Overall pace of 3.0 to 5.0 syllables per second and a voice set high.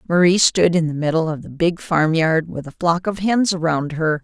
No: 4.9 syllables/s; medium, 165 Hz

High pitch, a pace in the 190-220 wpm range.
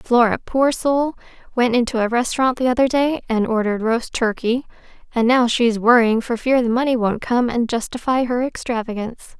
No: high, 240 Hz; average, 180 wpm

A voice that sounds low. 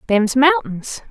No: very high, 250 Hz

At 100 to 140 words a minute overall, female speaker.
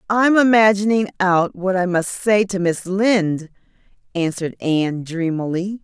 Yes: slow, 135 wpm; female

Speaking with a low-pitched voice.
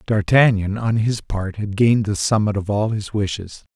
Yes: low, 105 Hz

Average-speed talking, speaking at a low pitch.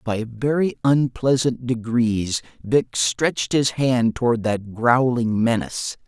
No: slow, 120 wpm; low, 120 Hz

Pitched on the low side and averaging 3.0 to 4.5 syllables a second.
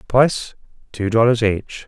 Yes: low, 115 Hz; 4.4 syllables/s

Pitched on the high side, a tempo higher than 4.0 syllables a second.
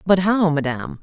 No: medium, 170 Hz; 5.5 syllables/s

